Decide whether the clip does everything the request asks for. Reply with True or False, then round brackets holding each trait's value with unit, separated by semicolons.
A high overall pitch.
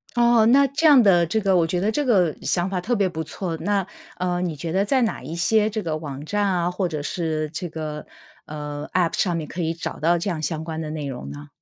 False (175 Hz)